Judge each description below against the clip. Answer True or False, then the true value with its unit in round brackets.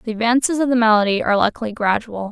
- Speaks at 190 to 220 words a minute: True (205 wpm)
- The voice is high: True (225 Hz)